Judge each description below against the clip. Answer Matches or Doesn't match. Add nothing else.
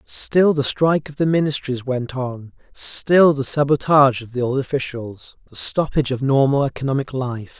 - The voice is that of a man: Matches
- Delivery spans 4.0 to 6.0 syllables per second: Matches